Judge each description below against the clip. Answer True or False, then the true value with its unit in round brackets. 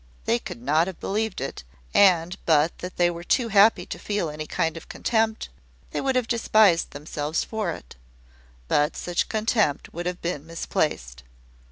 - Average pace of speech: True (170 wpm)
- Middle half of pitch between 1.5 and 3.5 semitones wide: False (5.6 semitones)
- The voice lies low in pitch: False (175 Hz)